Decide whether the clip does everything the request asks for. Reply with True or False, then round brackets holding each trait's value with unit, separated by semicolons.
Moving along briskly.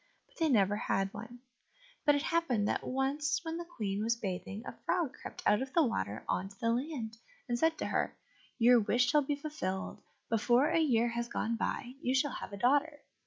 True (210 wpm)